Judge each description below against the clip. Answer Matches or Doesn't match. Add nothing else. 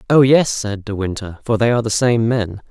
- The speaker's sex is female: Doesn't match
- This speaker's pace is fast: Matches